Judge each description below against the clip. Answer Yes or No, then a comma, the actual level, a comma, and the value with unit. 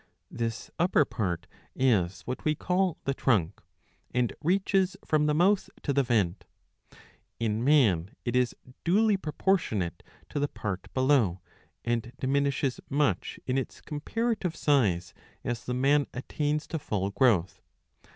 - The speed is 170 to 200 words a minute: No, average, 140 wpm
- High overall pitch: No, low, 130 Hz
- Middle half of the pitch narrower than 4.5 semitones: No, wide, 5.6 semitones